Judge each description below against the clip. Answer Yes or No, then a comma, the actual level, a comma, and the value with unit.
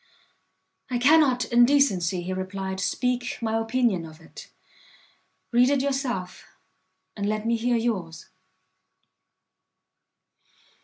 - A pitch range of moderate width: Yes, average, 4.8 semitones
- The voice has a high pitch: Yes, high, 230 Hz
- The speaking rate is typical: No, slow, 105 wpm